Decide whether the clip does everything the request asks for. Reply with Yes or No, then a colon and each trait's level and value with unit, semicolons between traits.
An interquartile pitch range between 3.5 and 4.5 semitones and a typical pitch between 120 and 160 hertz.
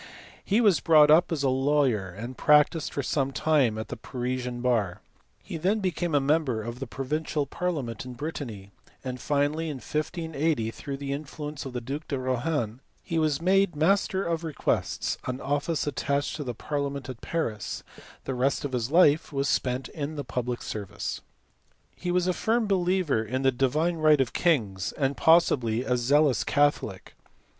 Yes: average, 4.0 semitones; medium, 140 Hz